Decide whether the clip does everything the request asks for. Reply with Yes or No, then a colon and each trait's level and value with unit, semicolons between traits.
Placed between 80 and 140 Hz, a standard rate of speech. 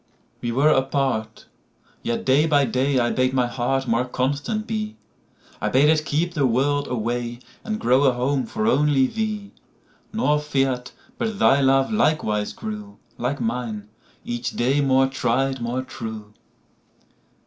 No: low, 135 Hz; slow, 130 wpm